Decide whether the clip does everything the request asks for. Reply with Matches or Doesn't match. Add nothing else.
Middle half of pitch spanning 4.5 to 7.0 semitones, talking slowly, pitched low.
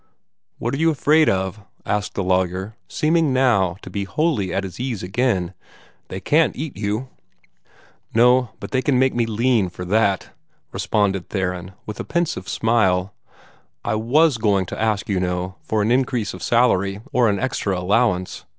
Doesn't match